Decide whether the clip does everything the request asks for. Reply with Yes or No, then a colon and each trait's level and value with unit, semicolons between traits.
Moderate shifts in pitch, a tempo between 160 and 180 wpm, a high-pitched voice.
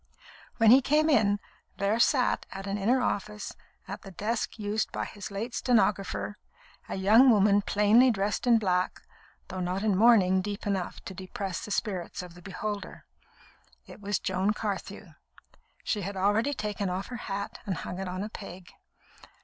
No: narrow, 2.3 semitones; average, 170 wpm; high, 205 Hz